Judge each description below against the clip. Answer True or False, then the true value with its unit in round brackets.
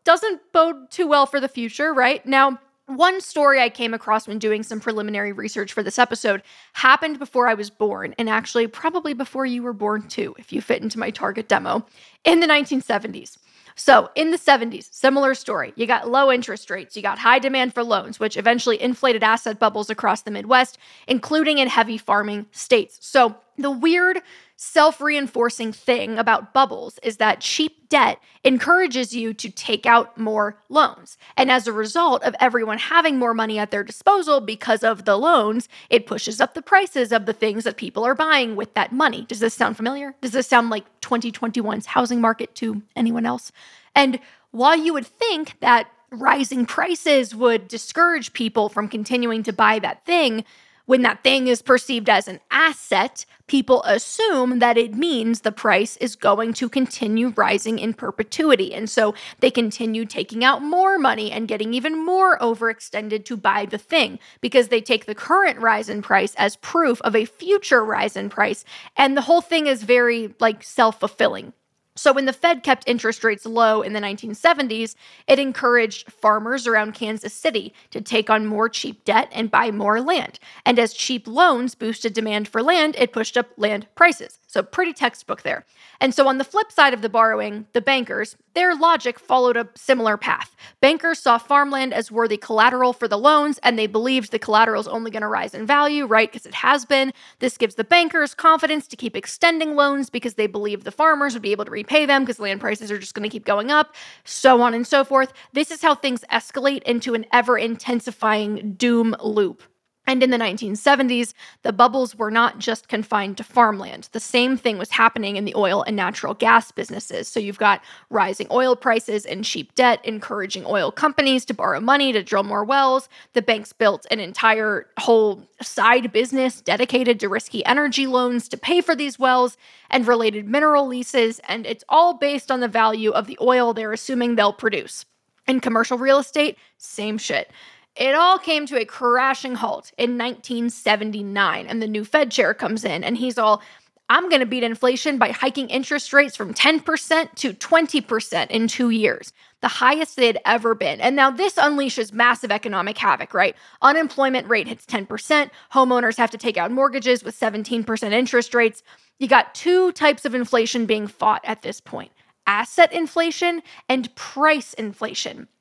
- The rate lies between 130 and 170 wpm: False (185 wpm)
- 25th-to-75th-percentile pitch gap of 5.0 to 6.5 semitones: False (3.8 semitones)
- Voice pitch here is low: False (240 Hz)